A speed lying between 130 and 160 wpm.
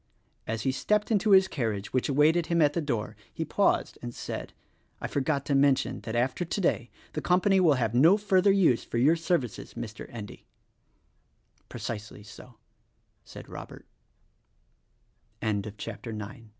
Yes: slow, 135 wpm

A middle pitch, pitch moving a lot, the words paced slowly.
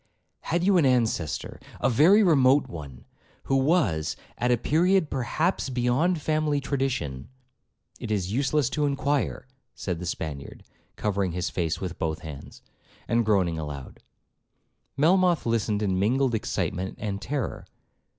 No: low, 120 Hz; wide, 7.9 semitones; slow, 130 wpm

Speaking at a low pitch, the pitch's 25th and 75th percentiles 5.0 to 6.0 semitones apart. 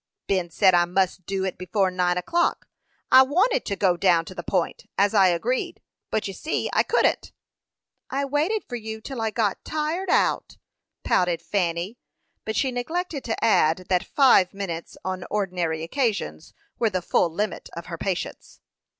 No: high, 195 Hz; wide, 5.6 semitones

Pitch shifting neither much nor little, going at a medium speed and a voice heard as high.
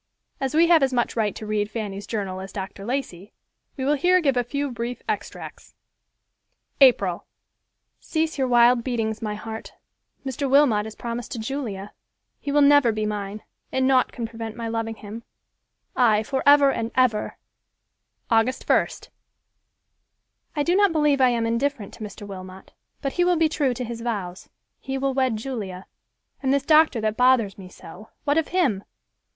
Yes: average, 4.4 semitones; average, 165 wpm; high, 240 Hz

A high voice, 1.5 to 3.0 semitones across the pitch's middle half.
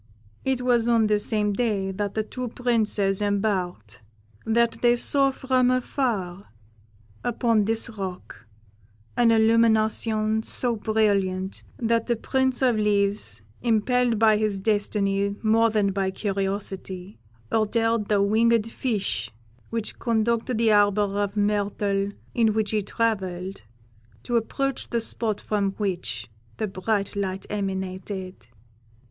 Yes: high, 215 Hz; narrow, 2.6 semitones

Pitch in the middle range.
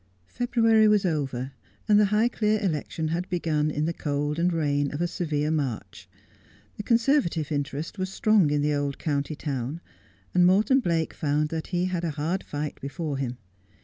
Yes: medium, 160 Hz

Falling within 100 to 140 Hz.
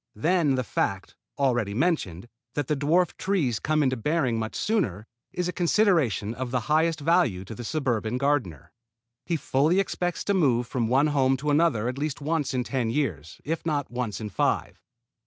Yes: low, 135 Hz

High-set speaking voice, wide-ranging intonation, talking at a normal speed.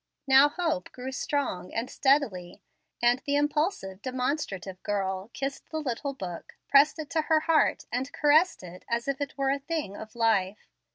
Yes: very high, 265 Hz; wide, 6.0 semitones; average, 170 wpm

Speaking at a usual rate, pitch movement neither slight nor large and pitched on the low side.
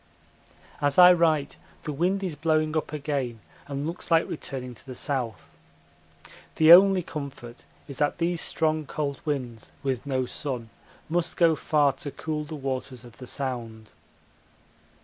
No: average, 150 wpm; average, 3.6 semitones; medium, 145 Hz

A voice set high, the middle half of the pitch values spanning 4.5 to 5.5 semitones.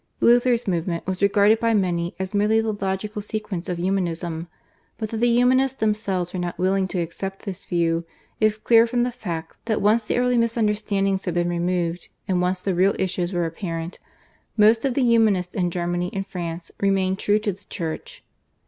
No: high, 195 Hz; average, 3.6 semitones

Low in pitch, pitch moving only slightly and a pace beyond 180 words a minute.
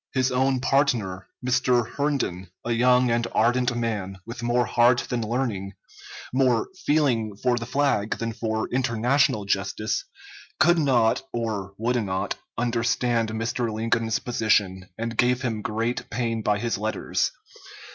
No: low, 115 Hz; narrow, 2.3 semitones; slow, 135 wpm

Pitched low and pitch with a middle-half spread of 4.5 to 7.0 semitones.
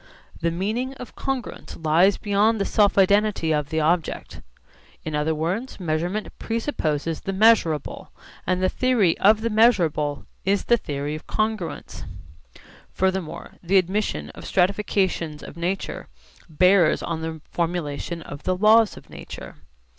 No: medium, 185 Hz; average, 4.8 semitones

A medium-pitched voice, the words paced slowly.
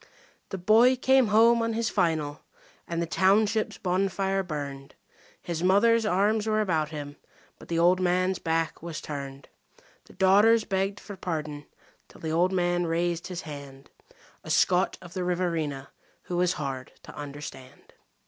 No: medium, 180 Hz; average, 155 wpm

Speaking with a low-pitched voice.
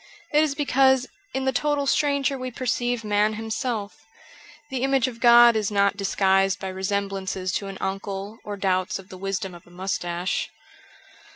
No: high, 205 Hz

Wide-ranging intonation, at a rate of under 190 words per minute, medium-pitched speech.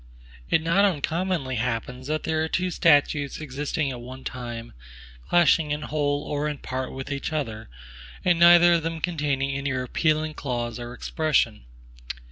No: average, 3.7 semitones; average, 155 wpm; medium, 145 Hz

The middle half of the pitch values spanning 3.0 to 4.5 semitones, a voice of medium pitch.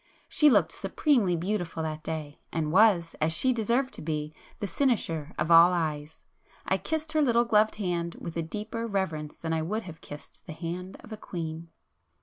No: average, 5.3 semitones; medium, 170 Hz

